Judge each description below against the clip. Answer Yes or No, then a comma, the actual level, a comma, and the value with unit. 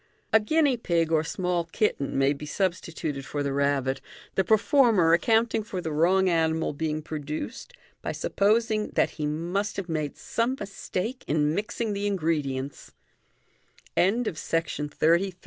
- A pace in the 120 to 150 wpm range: Yes, slow, 135 wpm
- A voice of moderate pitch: Yes, medium, 170 Hz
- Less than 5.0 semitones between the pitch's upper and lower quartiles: No, wide, 5.4 semitones